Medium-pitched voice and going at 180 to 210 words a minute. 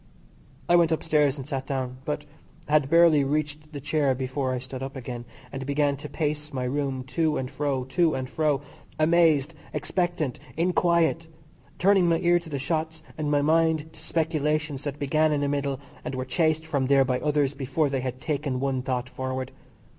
Yes: medium, 145 Hz; average, 185 wpm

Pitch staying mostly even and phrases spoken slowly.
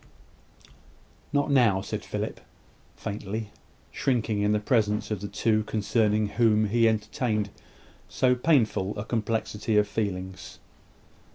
Yes: narrow, 1.8 semitones; slow, 115 wpm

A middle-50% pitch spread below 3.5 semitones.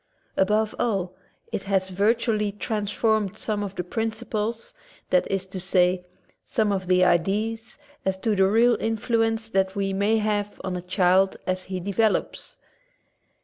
Yes: average, 2.7 semitones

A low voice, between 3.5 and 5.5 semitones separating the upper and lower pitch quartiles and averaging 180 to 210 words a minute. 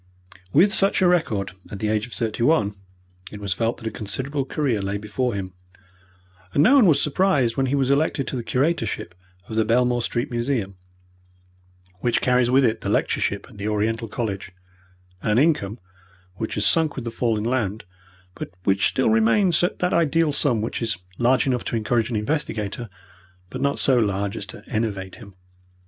Yes: low, 115 Hz; average, 4.6 semitones; average, 190 wpm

